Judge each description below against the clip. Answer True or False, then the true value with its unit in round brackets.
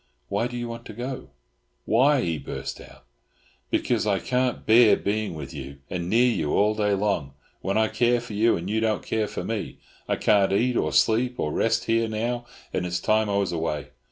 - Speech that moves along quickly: True (210 wpm)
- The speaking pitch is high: False (110 Hz)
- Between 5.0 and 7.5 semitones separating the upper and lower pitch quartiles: False (3.4 semitones)